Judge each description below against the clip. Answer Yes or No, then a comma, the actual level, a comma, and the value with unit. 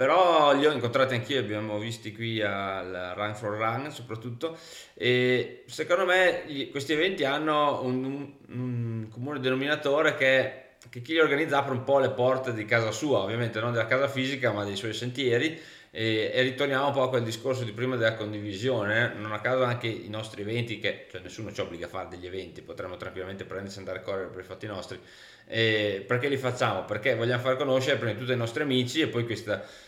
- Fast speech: Yes, fast, 210 wpm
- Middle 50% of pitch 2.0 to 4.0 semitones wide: Yes, average, 3.6 semitones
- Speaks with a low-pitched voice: Yes, low, 125 Hz